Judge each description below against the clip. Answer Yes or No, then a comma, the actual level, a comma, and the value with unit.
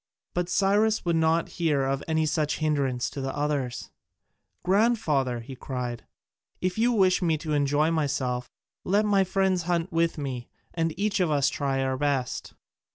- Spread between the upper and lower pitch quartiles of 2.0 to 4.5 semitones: No, average, 4.9 semitones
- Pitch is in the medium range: Yes, medium, 155 Hz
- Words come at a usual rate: Yes, average, 160 wpm